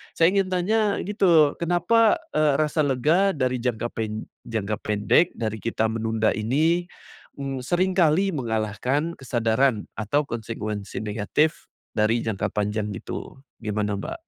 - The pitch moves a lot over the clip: Yes, wide, 7.3 semitones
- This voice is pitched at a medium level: No, low, 125 Hz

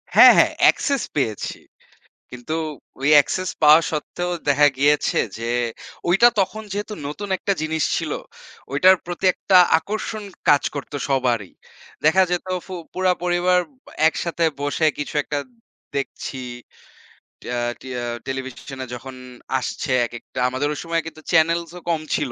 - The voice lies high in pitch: No, medium, 155 Hz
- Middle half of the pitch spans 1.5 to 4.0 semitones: No, average, 4.7 semitones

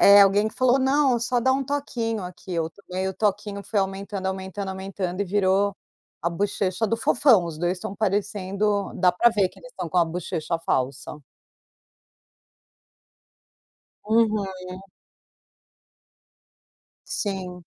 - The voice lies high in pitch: Yes, high, 195 Hz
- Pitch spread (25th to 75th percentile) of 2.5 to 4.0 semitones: Yes, average, 2.9 semitones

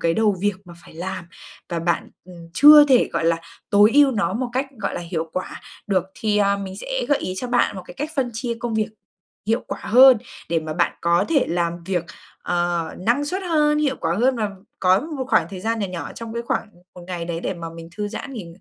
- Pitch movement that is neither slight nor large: No, wide, 6.3 semitones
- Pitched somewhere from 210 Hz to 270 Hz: No, high, 200 Hz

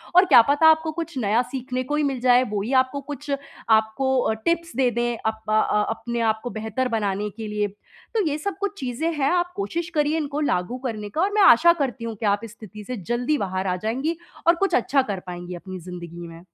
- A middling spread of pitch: No, wide, 6.1 semitones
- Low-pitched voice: No, very high, 250 Hz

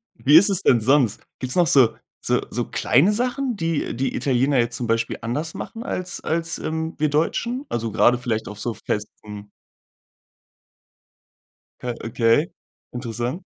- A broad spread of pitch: Yes, wide, 5.9 semitones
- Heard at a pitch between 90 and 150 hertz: Yes, low, 135 Hz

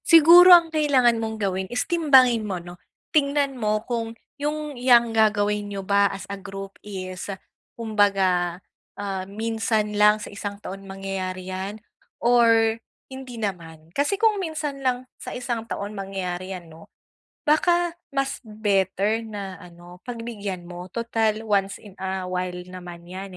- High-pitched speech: Yes, high, 210 Hz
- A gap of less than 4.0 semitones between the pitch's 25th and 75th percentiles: No, average, 4.3 semitones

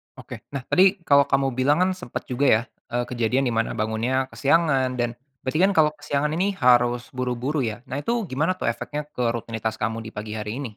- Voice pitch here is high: No, low, 130 Hz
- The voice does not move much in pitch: No, average, 3.7 semitones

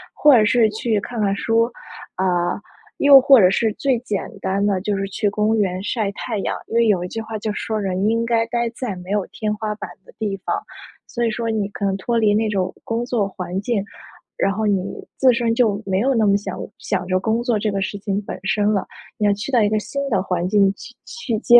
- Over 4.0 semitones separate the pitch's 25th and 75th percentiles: No, average, 2.8 semitones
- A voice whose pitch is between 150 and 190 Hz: No, high, 210 Hz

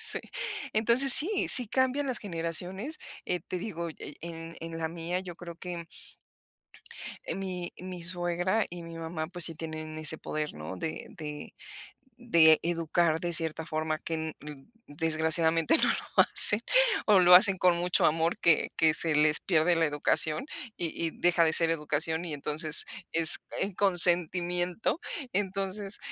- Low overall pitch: No, medium, 170 Hz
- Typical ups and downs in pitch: No, narrow, 2.3 semitones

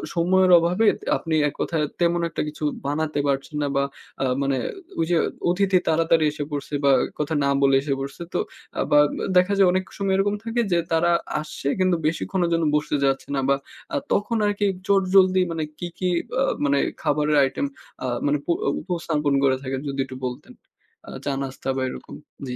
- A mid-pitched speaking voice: Yes, medium, 160 Hz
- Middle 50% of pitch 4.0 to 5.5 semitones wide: Yes, average, 4.7 semitones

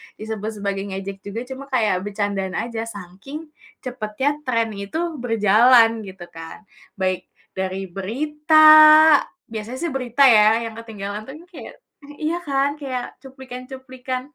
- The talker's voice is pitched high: Yes, high, 235 Hz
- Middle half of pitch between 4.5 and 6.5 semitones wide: Yes, average, 5.1 semitones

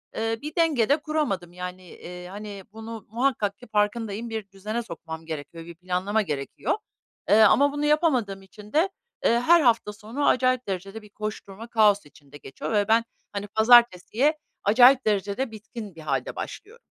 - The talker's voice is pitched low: No, high, 215 Hz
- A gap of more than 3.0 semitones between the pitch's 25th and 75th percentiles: Yes, average, 3.9 semitones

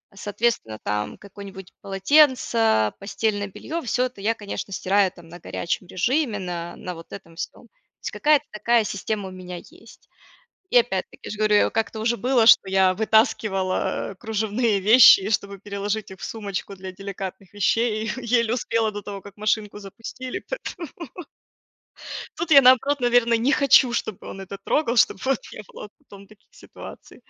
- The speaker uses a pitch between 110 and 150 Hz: No, high, 210 Hz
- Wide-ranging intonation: No, average, 3.5 semitones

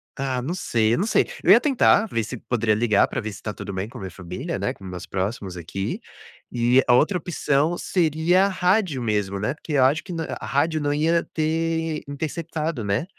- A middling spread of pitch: No, wide, 7.3 semitones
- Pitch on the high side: No, medium, 140 Hz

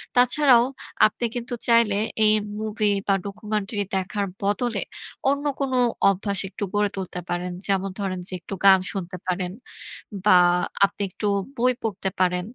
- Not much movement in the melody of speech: No, average, 3.0 semitones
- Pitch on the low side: No, high, 205 Hz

